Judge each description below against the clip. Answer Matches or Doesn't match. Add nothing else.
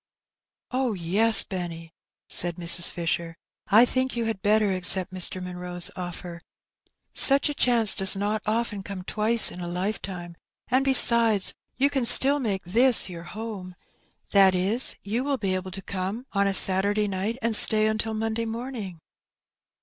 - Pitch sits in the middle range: Doesn't match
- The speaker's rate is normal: Matches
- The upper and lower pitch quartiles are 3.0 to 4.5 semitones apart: Matches